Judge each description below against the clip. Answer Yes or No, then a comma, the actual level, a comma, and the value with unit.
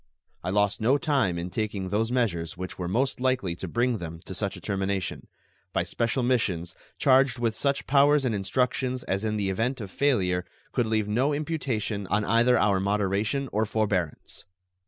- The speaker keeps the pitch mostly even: No, average, 4.7 semitones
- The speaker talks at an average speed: Yes, average, 175 wpm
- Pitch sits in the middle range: No, low, 110 Hz